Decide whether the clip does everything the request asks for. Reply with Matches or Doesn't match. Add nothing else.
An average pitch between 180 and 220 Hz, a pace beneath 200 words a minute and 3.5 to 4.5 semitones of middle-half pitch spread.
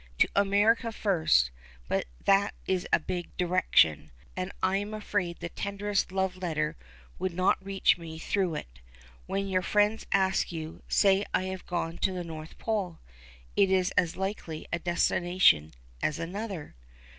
Doesn't match